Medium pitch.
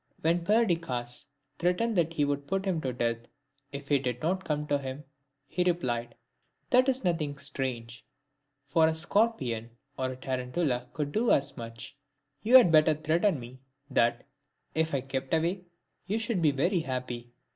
Yes: medium, 150 Hz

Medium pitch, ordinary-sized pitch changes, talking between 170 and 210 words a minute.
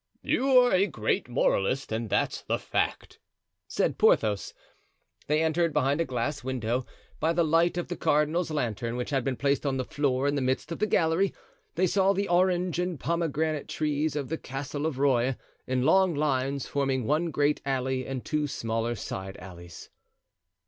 Yes: medium, 145 Hz; average, 4.3 semitones; average, 175 wpm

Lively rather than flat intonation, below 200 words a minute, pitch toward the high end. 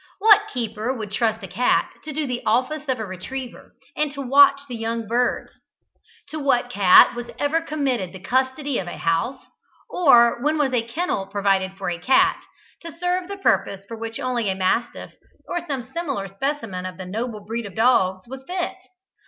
Yes: wide, 5.8 semitones; average, 185 wpm; high, 245 Hz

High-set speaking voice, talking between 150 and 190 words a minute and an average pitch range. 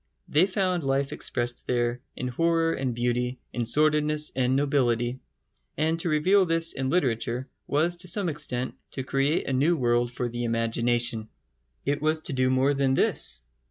No: low, 135 Hz; average, 165 wpm; average, 4.3 semitones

